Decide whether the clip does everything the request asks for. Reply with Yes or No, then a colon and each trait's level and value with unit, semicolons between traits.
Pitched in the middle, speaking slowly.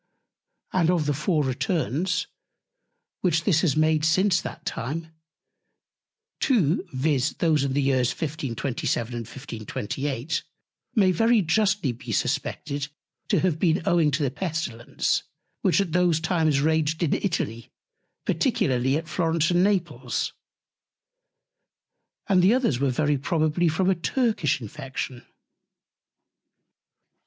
Yes: medium, 155 Hz; slow, 120 wpm